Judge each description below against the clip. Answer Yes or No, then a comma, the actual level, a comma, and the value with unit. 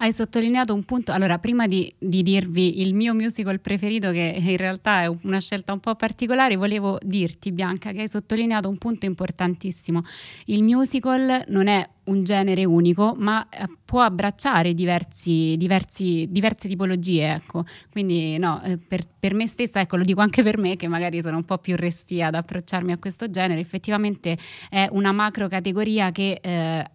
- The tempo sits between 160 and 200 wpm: Yes, fast, 170 wpm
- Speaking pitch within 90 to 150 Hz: No, high, 190 Hz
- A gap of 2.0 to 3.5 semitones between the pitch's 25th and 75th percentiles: Yes, average, 2.9 semitones